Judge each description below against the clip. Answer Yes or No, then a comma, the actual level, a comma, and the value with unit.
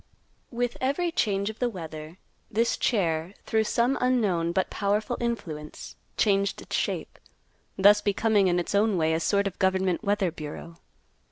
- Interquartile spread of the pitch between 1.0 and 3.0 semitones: No, average, 4.4 semitones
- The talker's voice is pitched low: No, high, 200 Hz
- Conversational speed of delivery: Yes, average, 155 wpm